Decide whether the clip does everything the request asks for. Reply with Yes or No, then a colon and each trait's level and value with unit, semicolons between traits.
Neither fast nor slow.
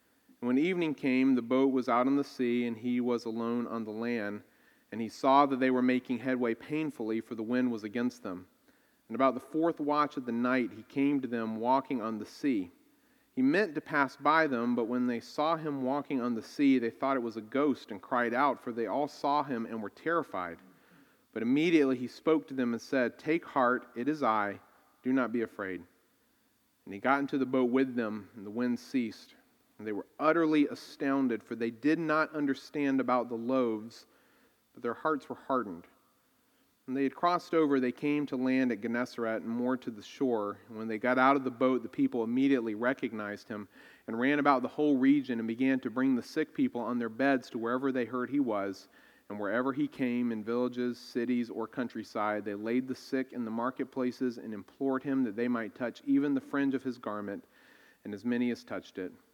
No: fast, 215 wpm